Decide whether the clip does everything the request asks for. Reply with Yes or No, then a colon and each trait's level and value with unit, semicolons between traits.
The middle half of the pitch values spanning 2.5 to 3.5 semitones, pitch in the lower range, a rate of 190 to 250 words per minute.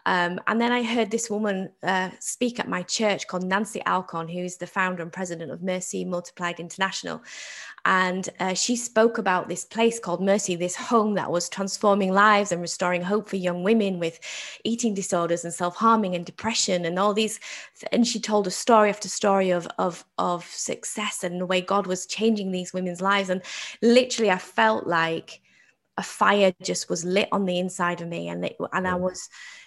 No: average, 2.9 semitones; high, 190 Hz; average, 195 wpm